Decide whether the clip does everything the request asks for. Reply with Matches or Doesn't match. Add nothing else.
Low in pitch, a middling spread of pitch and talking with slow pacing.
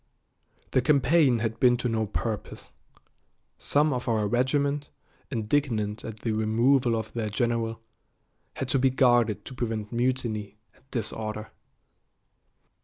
Matches